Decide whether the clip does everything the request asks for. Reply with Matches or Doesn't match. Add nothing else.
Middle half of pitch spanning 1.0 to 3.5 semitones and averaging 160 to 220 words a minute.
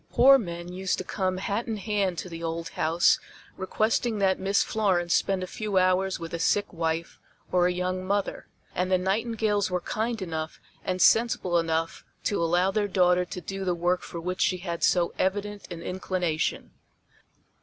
Matches